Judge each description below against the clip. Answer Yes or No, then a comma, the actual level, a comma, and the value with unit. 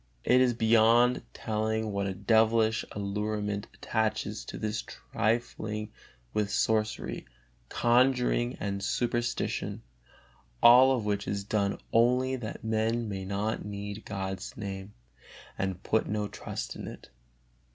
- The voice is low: Yes, low, 110 Hz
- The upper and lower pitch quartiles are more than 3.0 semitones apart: No, narrow, 2.4 semitones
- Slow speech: Yes, slow, 120 wpm